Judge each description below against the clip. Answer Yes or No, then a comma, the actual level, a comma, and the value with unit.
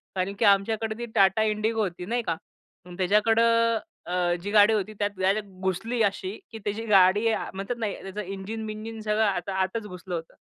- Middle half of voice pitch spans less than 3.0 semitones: Yes, narrow, 2.6 semitones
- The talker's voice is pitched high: Yes, high, 210 Hz